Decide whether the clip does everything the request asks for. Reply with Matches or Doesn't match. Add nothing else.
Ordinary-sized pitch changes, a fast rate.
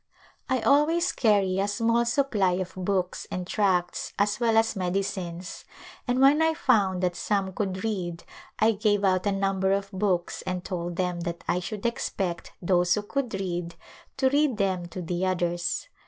Doesn't match